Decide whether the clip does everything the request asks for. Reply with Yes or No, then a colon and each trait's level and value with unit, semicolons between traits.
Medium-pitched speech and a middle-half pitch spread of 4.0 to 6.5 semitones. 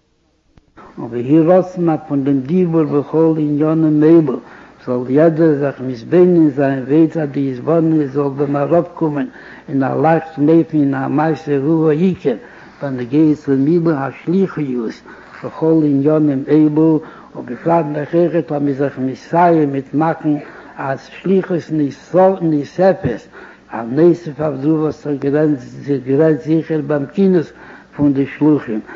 No: medium, 150 Hz; narrow, 2.5 semitones